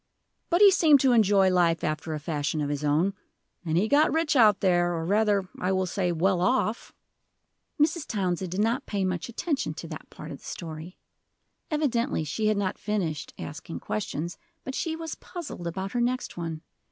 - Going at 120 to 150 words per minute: No, average, 190 wpm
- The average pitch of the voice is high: Yes, high, 195 Hz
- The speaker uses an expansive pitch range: Yes, wide, 6.3 semitones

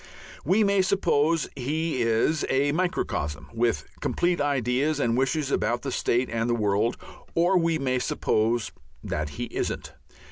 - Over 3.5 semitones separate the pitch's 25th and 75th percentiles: Yes, wide, 5.4 semitones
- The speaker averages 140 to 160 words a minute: Yes, average, 145 wpm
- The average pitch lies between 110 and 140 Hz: Yes, low, 135 Hz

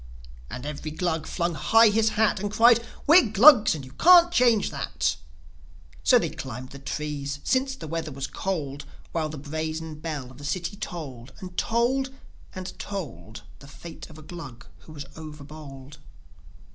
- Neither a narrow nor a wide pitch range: No, wide, 6.5 semitones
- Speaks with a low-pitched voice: No, medium, 160 Hz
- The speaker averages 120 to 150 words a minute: No, average, 170 wpm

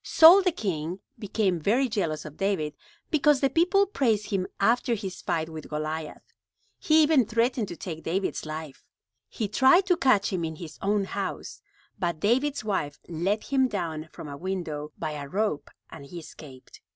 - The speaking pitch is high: Yes, high, 195 Hz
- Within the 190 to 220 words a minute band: No, average, 175 wpm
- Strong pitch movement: Yes, wide, 7.5 semitones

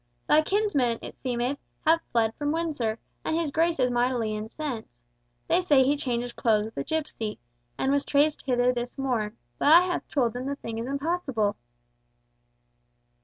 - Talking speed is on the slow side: No, average, 170 wpm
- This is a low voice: No, very high, 260 Hz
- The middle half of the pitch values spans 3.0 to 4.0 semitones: No, average, 4.6 semitones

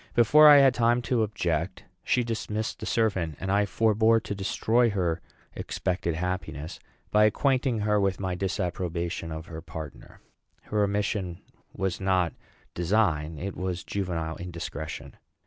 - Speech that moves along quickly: No, average, 140 wpm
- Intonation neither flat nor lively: Yes, average, 4.1 semitones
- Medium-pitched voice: No, very low, 95 Hz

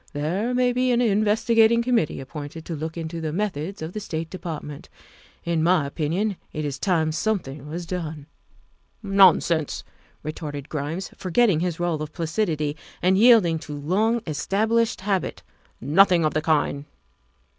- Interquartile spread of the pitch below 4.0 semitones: No, average, 5.0 semitones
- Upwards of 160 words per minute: Yes, average, 170 wpm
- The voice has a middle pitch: Yes, medium, 170 Hz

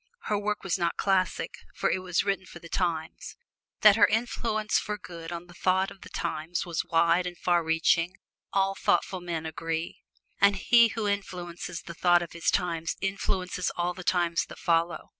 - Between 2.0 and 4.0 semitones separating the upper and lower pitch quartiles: Yes, narrow, 2.5 semitones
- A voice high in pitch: No, medium, 180 Hz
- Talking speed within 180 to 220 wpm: Yes, average, 185 wpm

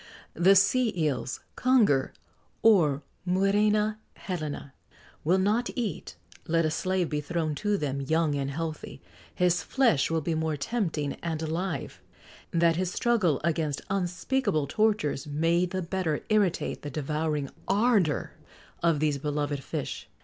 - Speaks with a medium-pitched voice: Yes, medium, 165 Hz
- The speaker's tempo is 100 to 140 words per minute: Yes, slow, 135 wpm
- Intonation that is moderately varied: Yes, average, 4.7 semitones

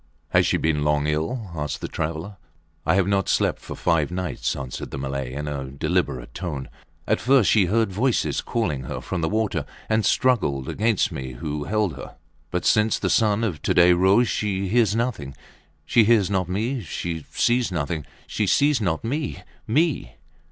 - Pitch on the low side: Yes, very low, 95 Hz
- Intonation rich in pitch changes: Yes, wide, 6.8 semitones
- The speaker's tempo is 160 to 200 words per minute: Yes, average, 180 wpm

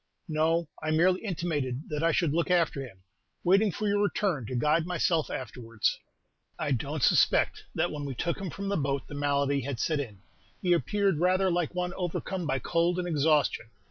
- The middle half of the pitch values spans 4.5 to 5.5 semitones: No, average, 4.1 semitones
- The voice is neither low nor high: Yes, medium, 160 Hz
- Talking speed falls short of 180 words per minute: No, average, 190 wpm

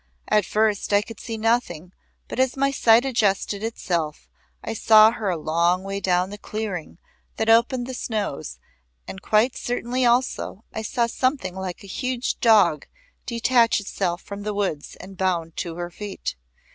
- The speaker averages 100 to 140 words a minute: No, average, 165 wpm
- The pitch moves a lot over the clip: No, average, 4.1 semitones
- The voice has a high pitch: Yes, high, 210 Hz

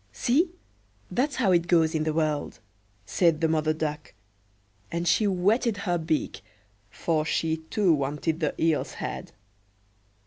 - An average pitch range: Yes, average, 3.0 semitones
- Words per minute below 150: Yes, average, 140 wpm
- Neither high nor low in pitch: Yes, medium, 165 Hz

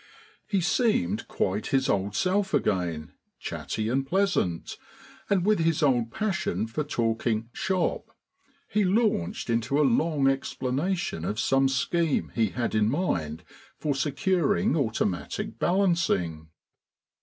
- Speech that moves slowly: Yes, slow, 120 wpm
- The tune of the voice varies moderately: No, wide, 8.8 semitones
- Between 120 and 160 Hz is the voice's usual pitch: Yes, low, 135 Hz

